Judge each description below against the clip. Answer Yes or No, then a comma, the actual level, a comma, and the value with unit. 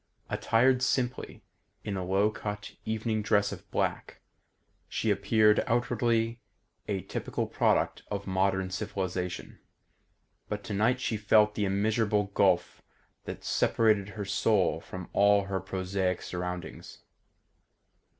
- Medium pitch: No, low, 105 Hz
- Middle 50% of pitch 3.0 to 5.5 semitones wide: No, narrow, 2.4 semitones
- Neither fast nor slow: No, slow, 115 wpm